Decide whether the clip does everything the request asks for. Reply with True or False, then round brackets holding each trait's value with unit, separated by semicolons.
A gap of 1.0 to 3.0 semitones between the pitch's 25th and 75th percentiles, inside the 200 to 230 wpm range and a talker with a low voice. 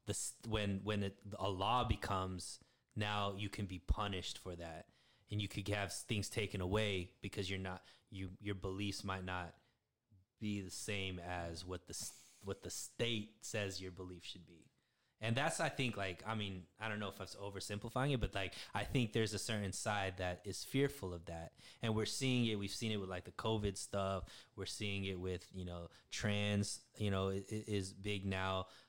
True (2.5 semitones; 205 wpm; 100 Hz)